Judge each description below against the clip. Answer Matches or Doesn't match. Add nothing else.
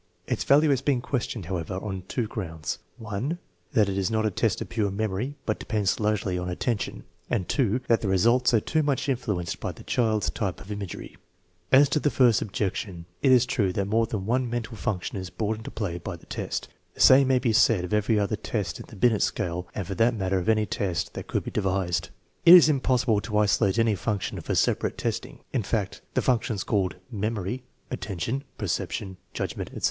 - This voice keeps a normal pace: Doesn't match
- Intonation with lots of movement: Doesn't match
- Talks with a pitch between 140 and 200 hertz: Doesn't match